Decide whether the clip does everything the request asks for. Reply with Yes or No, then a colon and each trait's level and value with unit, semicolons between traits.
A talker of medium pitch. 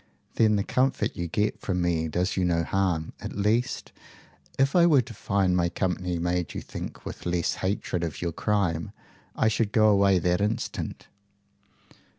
No: very low, 95 Hz